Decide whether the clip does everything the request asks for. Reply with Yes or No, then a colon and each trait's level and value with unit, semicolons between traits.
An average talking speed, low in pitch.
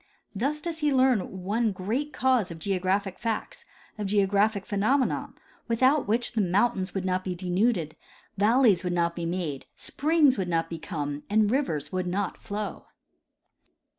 No: average, 155 wpm; high, 200 Hz